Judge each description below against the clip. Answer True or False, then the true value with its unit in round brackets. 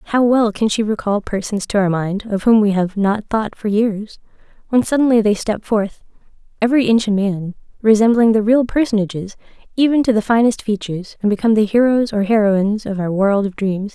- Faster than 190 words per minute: True (200 wpm)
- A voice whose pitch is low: False (215 Hz)